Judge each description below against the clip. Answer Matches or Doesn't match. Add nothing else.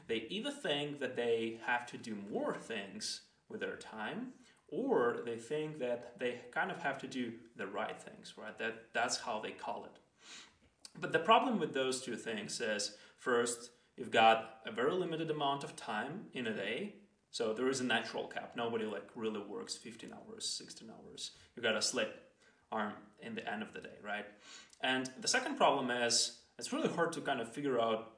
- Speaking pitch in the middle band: Doesn't match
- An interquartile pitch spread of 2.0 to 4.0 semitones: Doesn't match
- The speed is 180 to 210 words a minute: Matches